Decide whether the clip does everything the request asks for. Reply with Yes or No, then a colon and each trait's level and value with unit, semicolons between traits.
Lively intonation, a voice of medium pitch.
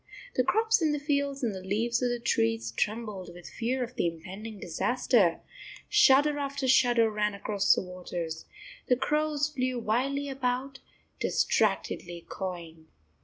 No: wide, 6.6 semitones; high, 235 Hz